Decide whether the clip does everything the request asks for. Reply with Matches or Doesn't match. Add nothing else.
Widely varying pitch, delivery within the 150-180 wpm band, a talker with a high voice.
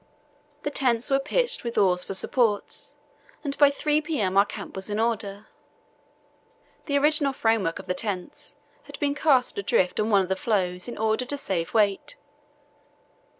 Matches